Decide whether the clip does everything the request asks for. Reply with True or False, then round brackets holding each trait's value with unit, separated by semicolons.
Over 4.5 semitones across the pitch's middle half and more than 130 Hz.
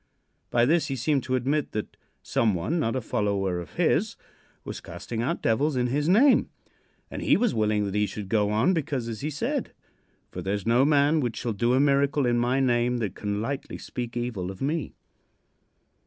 False (4.9 semitones; 120 Hz)